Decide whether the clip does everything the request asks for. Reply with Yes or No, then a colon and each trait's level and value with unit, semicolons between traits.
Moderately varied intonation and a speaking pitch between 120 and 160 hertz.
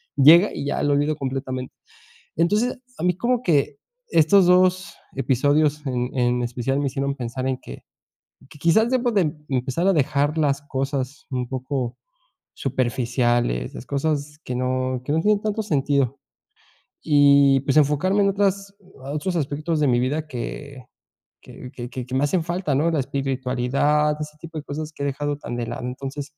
Yes: average, 3.7 semitones; medium, 140 Hz